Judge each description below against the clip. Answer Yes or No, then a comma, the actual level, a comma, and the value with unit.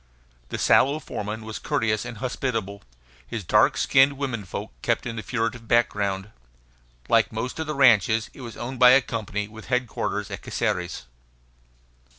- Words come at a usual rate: Yes, average, 160 wpm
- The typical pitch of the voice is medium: No, low, 115 Hz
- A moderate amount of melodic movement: Yes, average, 3.1 semitones